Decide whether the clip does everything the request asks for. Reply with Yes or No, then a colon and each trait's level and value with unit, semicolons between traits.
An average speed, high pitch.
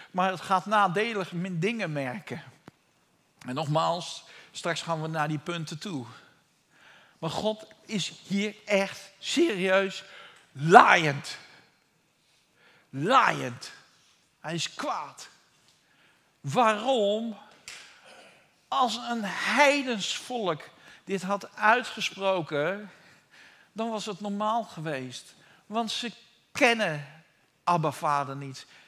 No: slow, 90 wpm; high, 195 Hz